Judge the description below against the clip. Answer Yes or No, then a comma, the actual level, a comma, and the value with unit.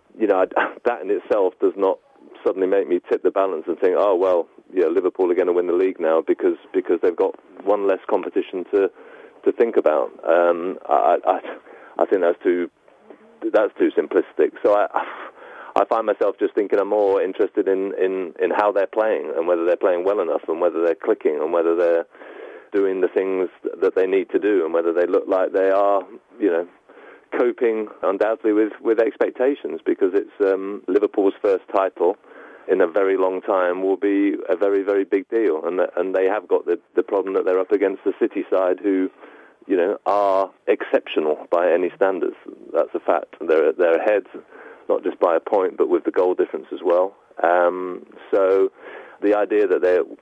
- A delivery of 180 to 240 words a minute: Yes, average, 195 wpm